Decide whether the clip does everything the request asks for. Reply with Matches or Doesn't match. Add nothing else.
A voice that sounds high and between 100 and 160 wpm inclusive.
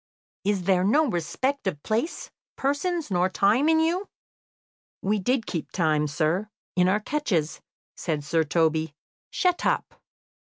Matches